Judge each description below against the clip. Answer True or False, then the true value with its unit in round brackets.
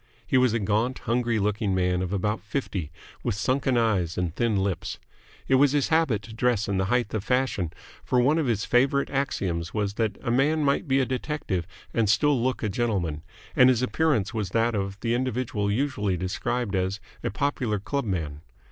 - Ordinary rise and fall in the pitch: True (4.7 semitones)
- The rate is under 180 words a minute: False (190 wpm)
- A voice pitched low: True (115 Hz)